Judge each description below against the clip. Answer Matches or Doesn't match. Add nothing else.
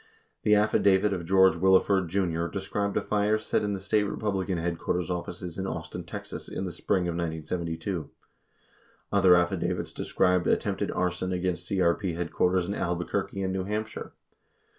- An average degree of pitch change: Doesn't match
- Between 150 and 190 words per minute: Matches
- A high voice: Doesn't match